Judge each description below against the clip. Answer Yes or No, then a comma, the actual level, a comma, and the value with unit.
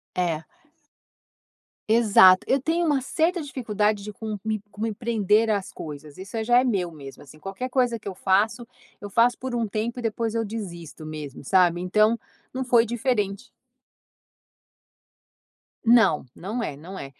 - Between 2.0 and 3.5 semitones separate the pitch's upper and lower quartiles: No, average, 4.3 semitones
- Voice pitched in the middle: No, high, 215 Hz